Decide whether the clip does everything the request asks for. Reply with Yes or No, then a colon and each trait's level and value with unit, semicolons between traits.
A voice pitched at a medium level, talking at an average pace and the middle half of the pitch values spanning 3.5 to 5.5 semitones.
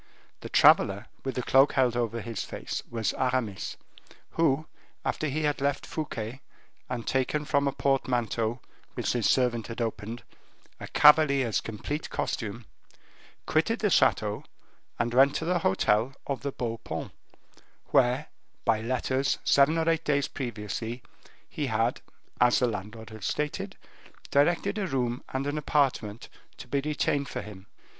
No: low, 130 Hz; average, 150 wpm; average, 3.8 semitones